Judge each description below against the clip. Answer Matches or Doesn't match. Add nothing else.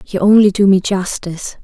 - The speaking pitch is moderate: Doesn't match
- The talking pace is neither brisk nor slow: Matches